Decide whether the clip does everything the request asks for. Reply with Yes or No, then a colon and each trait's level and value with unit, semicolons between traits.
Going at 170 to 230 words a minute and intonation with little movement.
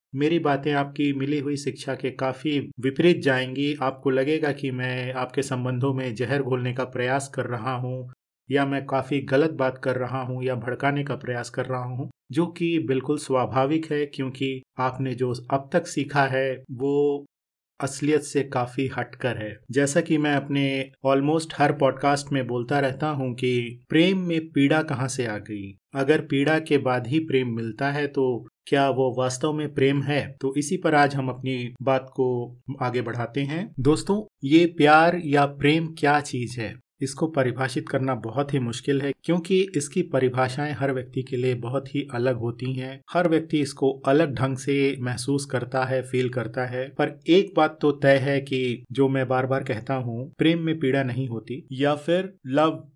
Yes: average, 185 wpm; narrow, 2.2 semitones